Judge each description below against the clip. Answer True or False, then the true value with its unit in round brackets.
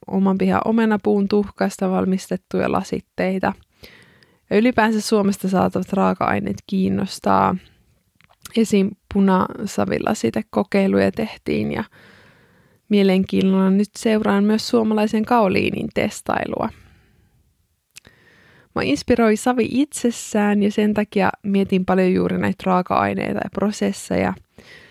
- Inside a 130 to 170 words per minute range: False (95 wpm)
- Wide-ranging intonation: True (7.2 semitones)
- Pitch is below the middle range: False (195 Hz)